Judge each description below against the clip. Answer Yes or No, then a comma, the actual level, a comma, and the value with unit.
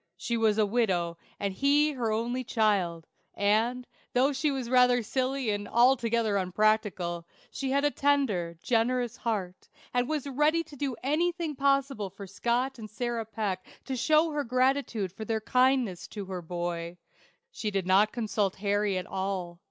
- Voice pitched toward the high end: Yes, high, 230 Hz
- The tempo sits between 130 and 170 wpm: Yes, average, 160 wpm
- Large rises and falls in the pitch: No, average, 5.0 semitones